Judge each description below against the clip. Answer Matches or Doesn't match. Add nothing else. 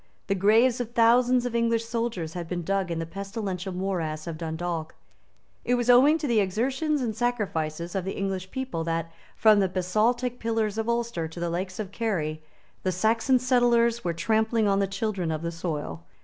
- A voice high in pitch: Matches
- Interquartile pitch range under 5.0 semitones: Doesn't match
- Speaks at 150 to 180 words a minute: Doesn't match